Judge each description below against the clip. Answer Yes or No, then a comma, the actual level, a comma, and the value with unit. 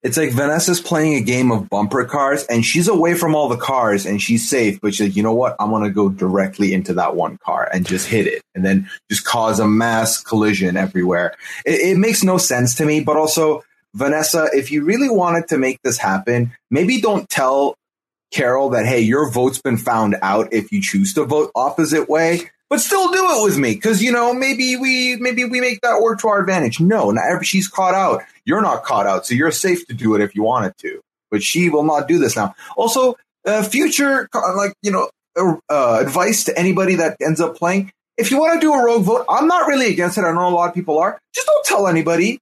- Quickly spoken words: Yes, fast, 235 wpm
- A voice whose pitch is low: No, medium, 165 Hz